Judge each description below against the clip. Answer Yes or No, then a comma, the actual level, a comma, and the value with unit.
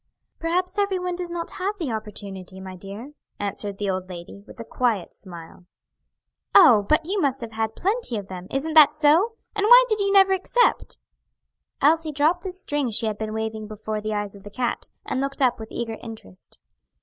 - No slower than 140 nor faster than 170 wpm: No, average, 195 wpm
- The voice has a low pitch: No, high, 240 Hz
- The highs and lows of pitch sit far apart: Yes, wide, 9.0 semitones